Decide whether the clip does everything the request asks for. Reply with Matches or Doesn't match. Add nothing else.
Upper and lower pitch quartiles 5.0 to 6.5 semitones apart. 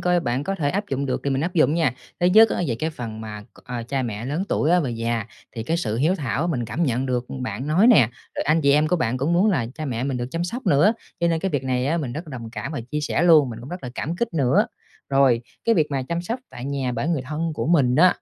Matches